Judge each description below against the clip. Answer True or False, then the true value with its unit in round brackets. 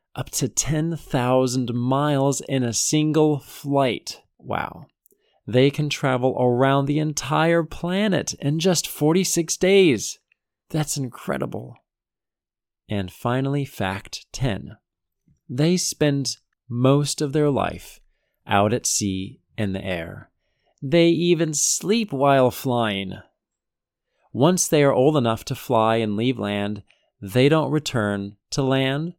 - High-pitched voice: False (135 Hz)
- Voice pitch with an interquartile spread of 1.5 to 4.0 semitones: False (5.2 semitones)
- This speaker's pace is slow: True (120 wpm)